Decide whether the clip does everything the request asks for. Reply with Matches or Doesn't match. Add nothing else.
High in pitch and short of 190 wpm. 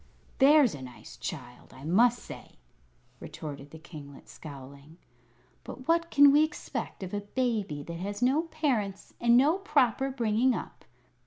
Matches